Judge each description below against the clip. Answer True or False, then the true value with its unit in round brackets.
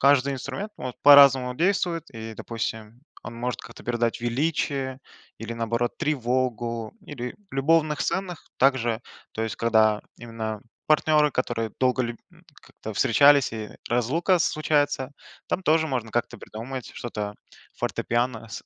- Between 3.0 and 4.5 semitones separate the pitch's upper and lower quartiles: True (3.9 semitones)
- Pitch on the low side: True (125 Hz)